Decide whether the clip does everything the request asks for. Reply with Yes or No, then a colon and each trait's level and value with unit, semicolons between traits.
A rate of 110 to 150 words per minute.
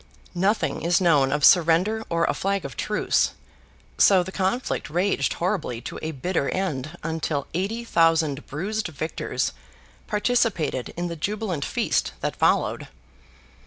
Yes: slow, 135 wpm